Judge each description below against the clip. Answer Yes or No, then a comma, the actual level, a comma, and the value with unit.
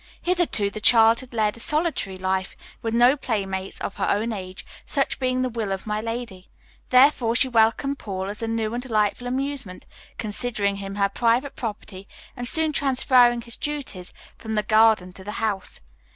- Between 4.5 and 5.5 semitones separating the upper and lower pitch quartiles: No, average, 3.9 semitones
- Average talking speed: Yes, average, 180 wpm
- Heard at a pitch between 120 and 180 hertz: No, high, 225 Hz